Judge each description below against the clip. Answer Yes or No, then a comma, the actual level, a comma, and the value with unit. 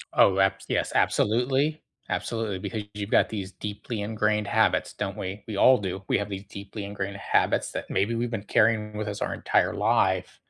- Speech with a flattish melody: Yes, narrow, 2.0 semitones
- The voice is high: No, low, 105 Hz